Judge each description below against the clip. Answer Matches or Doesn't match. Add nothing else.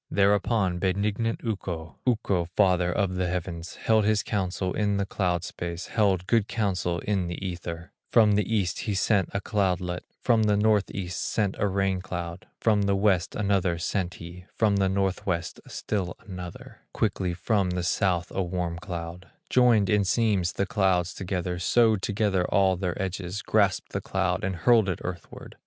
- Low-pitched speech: Matches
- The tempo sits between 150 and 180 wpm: Matches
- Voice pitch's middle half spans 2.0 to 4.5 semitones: Matches